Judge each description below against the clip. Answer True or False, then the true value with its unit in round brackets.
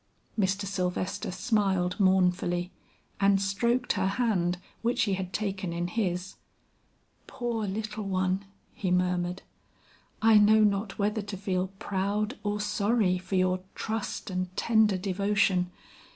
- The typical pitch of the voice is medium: False (195 Hz)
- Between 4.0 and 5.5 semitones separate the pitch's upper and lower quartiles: False (2.5 semitones)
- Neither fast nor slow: False (125 wpm)